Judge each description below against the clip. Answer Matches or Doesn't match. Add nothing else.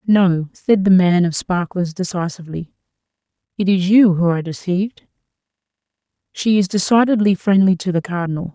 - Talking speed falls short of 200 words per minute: Matches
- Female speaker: Matches